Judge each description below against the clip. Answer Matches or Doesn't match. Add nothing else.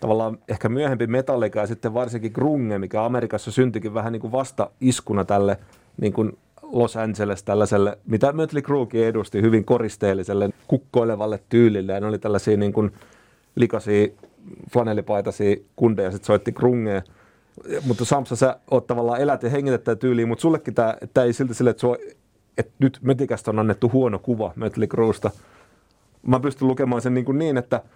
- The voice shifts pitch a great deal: Doesn't match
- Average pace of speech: Doesn't match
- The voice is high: Doesn't match